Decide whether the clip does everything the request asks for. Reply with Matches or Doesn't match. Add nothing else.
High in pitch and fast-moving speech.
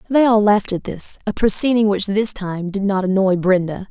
Matches